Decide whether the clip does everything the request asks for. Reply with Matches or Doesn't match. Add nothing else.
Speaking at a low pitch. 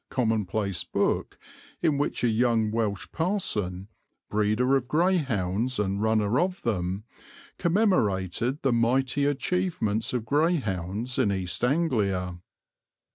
Matches